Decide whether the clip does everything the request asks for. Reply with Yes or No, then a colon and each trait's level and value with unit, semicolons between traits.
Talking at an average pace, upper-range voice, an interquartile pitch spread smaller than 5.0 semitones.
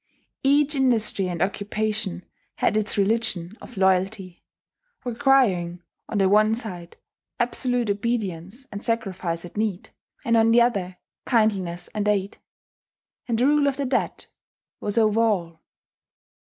No: slow, 130 wpm; high, 210 Hz; average, 3.8 semitones